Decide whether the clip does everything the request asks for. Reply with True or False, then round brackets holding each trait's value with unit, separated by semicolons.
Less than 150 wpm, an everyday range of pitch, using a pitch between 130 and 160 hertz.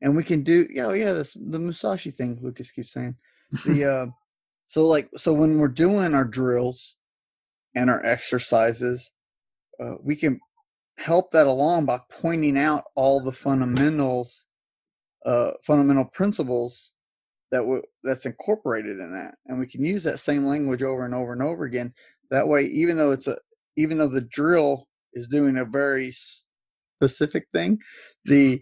False (165 wpm; 3.7 semitones; 140 Hz)